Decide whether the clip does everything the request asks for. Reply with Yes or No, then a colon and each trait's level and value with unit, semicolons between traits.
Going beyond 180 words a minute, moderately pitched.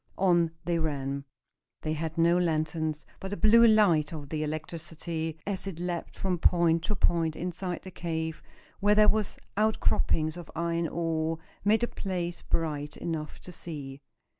No: average, 160 wpm; medium, 165 Hz